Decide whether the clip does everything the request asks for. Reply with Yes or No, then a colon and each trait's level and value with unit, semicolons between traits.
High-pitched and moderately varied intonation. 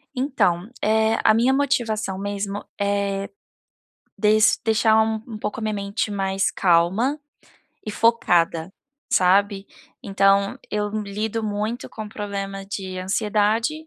No: high, 210 Hz; narrow, 2.0 semitones